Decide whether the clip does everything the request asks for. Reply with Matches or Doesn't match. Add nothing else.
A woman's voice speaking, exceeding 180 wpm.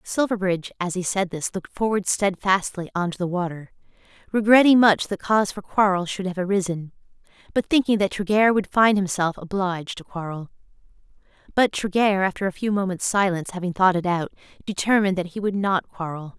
Doesn't match